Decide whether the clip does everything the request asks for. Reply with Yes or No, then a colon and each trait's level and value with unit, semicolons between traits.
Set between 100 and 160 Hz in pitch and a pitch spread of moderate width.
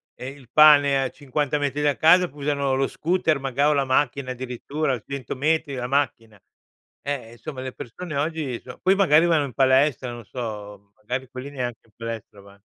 Yes: low, 135 Hz; average, 3.1 semitones